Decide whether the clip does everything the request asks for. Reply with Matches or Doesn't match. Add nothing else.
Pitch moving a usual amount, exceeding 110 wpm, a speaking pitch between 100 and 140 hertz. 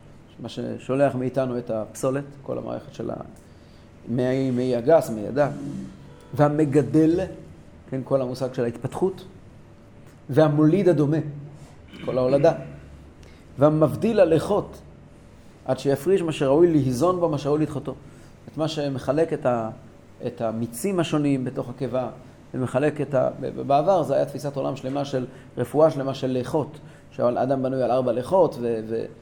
Matches